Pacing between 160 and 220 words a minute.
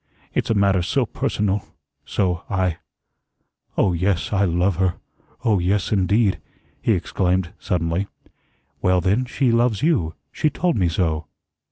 No: average, 140 wpm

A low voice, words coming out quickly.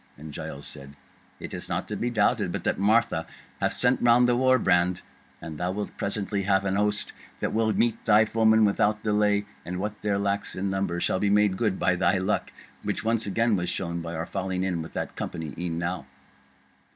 Yes: low, 100 Hz; fast, 210 wpm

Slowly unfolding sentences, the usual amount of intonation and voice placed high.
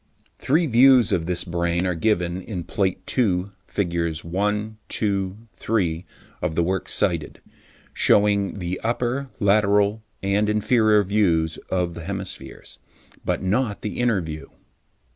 No: slow, 130 wpm; average, 3.5 semitones; low, 100 Hz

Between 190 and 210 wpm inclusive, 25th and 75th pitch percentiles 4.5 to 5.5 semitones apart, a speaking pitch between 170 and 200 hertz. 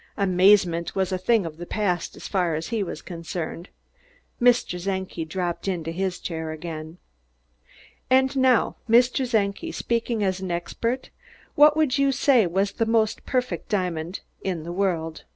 No: average, 150 wpm; average, 5.2 semitones; high, 190 Hz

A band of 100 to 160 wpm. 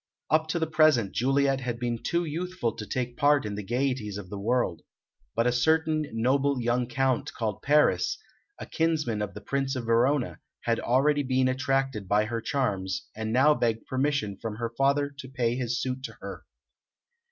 No: average, 185 wpm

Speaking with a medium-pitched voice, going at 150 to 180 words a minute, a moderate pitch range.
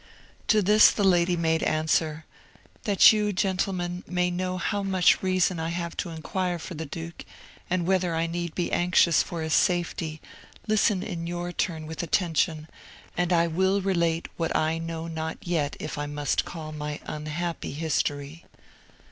No: medium, 170 Hz; average, 165 wpm; narrow, 2.3 semitones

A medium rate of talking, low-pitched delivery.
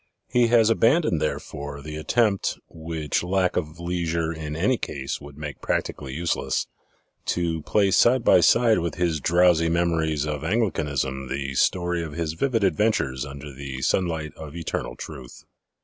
Yes: average, 150 wpm; very low, 80 Hz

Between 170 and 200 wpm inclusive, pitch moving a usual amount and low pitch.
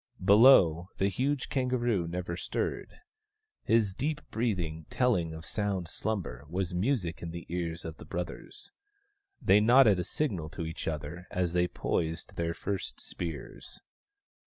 No: average, 140 wpm; average, 4.7 semitones; very low, 90 Hz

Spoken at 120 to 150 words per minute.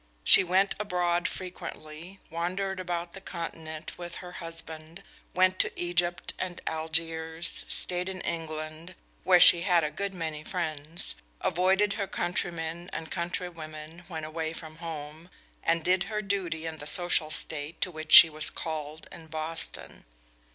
Yes: average, 145 wpm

